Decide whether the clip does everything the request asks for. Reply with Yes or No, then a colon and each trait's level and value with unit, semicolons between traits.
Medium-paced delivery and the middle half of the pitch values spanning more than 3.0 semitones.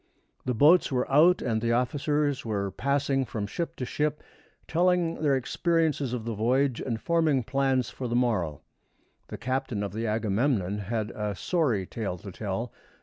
Yes: average, 165 wpm; average, 4.8 semitones